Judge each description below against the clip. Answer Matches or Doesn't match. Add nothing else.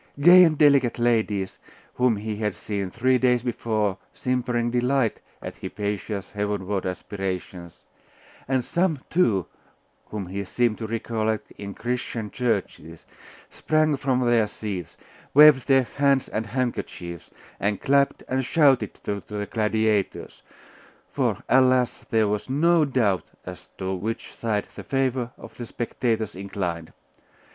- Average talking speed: Doesn't match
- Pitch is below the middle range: Matches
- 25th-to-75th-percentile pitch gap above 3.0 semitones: Matches